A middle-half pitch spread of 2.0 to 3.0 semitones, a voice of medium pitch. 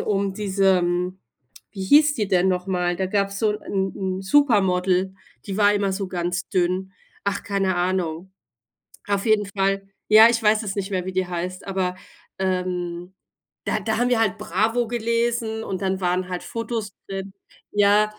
No: narrow, 2.4 semitones; high, 195 Hz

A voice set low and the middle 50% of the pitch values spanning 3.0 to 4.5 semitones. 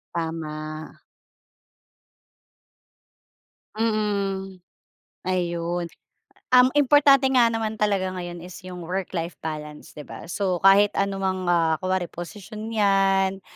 No: high, 190 Hz; average, 3.4 semitones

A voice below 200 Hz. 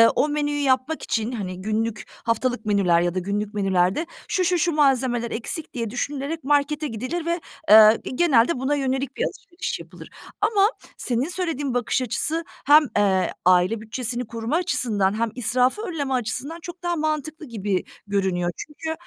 No: very high, 255 Hz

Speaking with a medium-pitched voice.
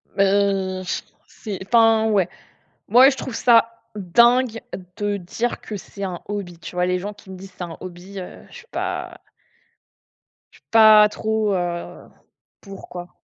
No: high, 200 Hz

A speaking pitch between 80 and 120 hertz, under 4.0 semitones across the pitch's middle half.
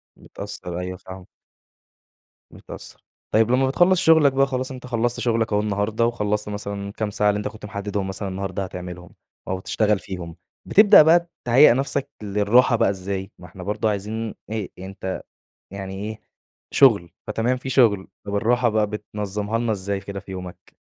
Yes: low, 105 Hz; average, 3.4 semitones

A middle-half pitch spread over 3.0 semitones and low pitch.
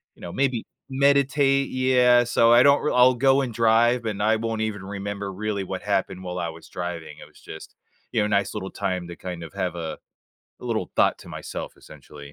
Yes: average, 5.2 semitones; low, 105 Hz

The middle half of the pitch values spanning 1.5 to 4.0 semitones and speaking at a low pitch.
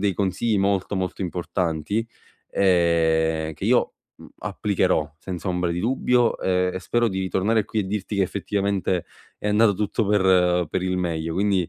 Yes: average, 2.7 semitones; very low, 95 Hz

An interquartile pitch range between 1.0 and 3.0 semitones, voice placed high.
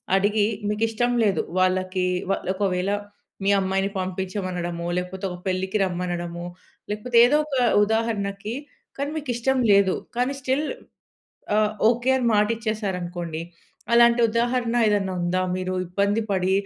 No: average, 3.7 semitones; high, 200 Hz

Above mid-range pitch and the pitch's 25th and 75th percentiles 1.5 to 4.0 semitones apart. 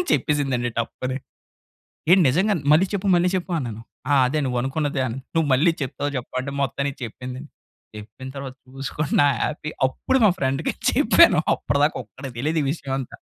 No: medium, 140 Hz; average, 3.3 semitones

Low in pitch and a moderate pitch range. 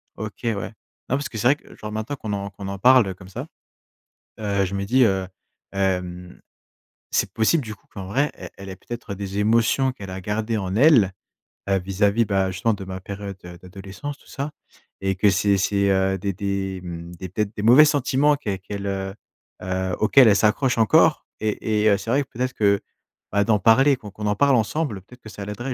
Yes: low, 100 Hz; average, 3.1 semitones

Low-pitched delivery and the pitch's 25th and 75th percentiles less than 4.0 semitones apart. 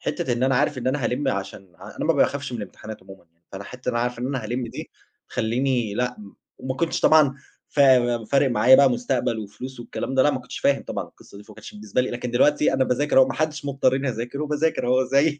Yes: low, 125 Hz; average, 2.7 semitones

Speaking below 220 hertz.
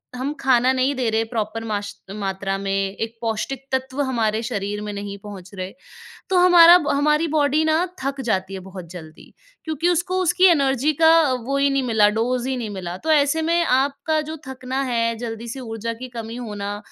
No: very high, 250 Hz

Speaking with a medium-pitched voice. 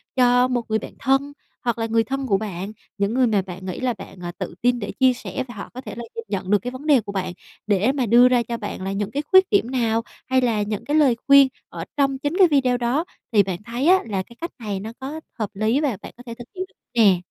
No: high, 235 Hz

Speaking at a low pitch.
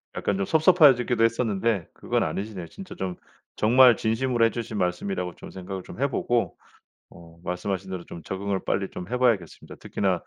Yes: low, 100 Hz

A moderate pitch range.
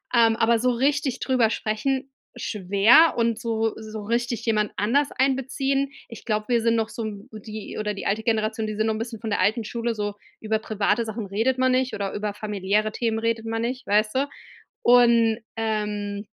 No: narrow, 2.1 semitones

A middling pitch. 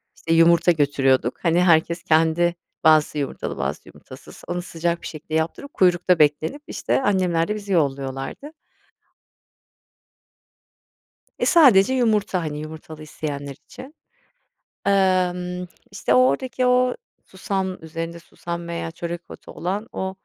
Yes: medium, 170 Hz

